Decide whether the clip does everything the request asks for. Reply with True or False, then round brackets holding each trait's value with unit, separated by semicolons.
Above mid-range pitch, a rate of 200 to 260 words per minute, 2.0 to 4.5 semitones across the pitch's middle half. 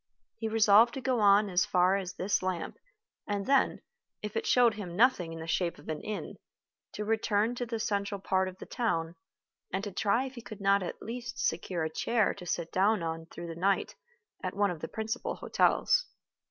True (200 Hz; 205 wpm; 3.8 semitones)